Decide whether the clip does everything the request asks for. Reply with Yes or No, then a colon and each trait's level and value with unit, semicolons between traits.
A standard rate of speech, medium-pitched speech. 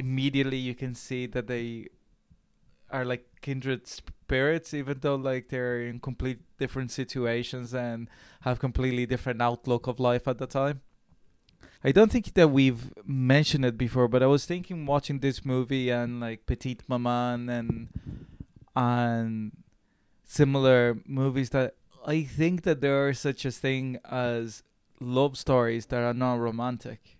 No: average, 150 wpm; low, 130 Hz